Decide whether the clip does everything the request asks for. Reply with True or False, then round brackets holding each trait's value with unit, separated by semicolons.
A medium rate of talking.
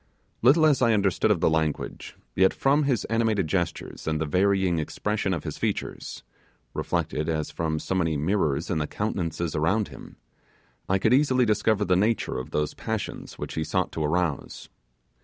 True (175 wpm)